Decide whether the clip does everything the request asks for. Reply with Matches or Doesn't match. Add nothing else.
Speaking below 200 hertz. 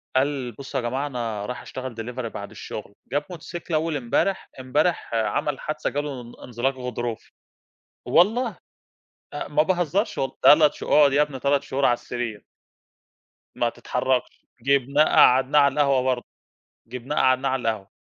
Matches